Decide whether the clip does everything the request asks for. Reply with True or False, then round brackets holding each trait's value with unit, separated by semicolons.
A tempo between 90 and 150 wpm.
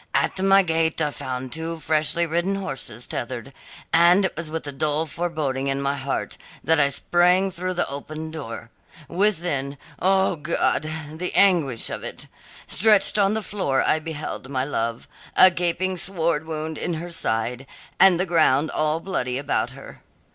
False (165 wpm)